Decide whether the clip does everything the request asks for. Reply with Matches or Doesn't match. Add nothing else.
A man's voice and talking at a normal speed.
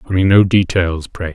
Matches